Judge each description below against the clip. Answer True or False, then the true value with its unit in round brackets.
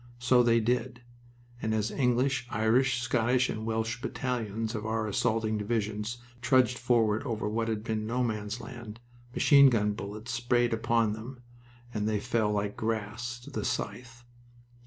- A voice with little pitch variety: True (2.1 semitones)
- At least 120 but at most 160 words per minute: True (155 wpm)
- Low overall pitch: True (115 Hz)